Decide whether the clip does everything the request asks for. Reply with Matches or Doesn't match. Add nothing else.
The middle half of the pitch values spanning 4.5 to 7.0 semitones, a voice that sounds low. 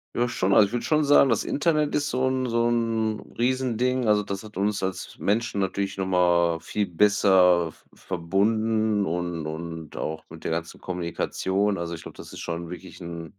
Matches